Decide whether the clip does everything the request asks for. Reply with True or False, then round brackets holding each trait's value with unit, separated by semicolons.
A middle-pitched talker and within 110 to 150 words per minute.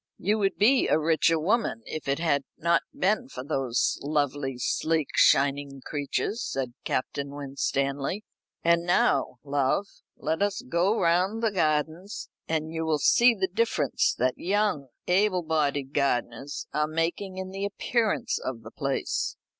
True (160 Hz; 145 wpm)